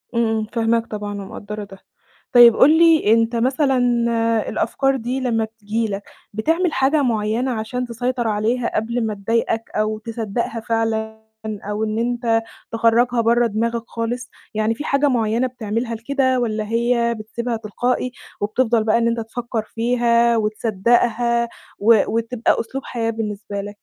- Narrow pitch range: Yes, narrow, 1.8 semitones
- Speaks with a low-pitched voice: No, high, 230 Hz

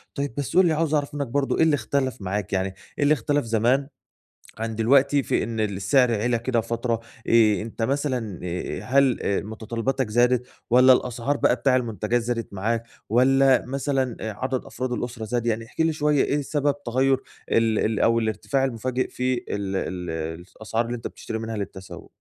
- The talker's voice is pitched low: Yes, low, 120 Hz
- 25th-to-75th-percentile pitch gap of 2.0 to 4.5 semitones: Yes, average, 3.5 semitones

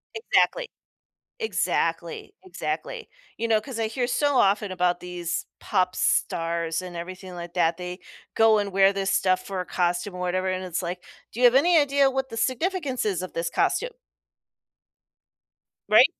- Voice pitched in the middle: No, high, 195 Hz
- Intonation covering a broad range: Yes, wide, 6.5 semitones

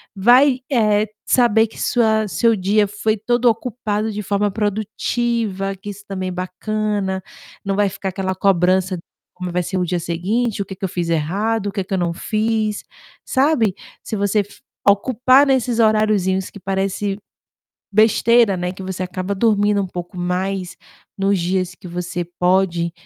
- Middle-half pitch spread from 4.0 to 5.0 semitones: No, average, 2.8 semitones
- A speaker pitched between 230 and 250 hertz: No, high, 200 Hz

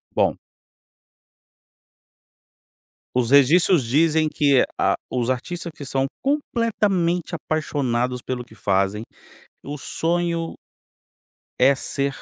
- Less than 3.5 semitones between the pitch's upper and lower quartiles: No, average, 5.0 semitones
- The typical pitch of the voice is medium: Yes, medium, 145 Hz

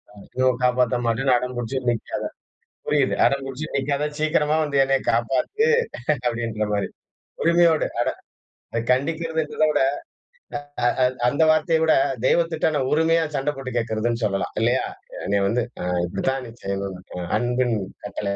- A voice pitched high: No, low, 130 Hz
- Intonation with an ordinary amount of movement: Yes, average, 4.7 semitones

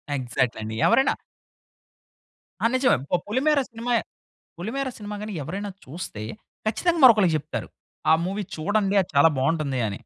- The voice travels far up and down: Yes, wide, 7.2 semitones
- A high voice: Yes, high, 200 Hz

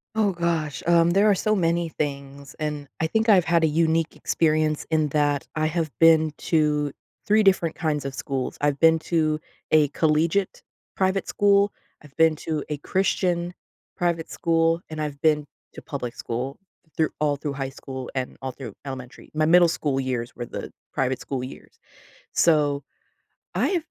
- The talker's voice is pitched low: No, medium, 155 Hz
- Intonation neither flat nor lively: Yes, average, 3.1 semitones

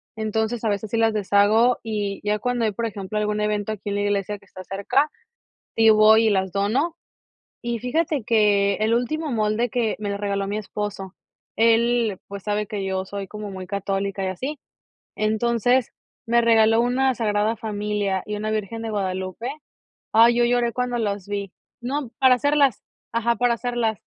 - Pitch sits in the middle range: No, high, 215 Hz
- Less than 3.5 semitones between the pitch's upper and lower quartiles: Yes, average, 2.7 semitones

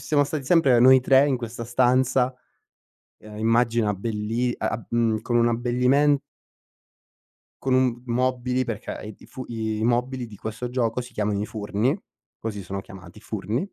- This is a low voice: Yes, low, 120 Hz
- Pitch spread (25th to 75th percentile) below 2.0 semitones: No, average, 2.7 semitones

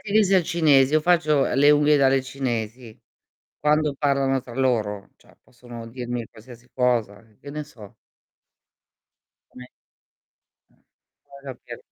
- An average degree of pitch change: Yes, average, 3.7 semitones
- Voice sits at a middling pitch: No, low, 130 Hz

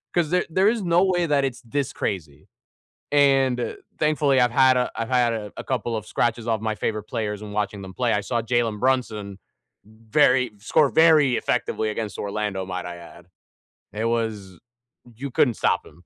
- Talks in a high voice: No, low, 115 Hz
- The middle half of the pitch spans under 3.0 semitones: No, average, 4.3 semitones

